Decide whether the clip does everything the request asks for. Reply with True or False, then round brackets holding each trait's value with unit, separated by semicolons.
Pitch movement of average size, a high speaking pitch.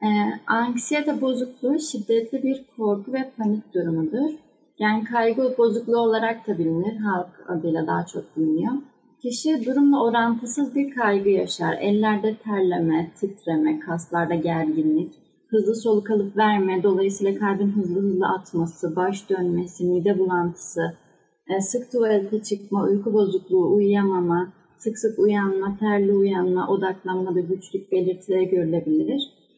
True (4.1 semitones; 205 Hz)